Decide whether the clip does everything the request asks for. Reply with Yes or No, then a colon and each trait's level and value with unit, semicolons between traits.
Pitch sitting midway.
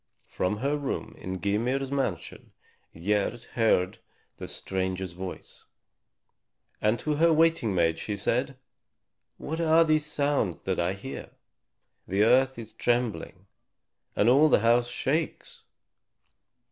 No: low, 120 Hz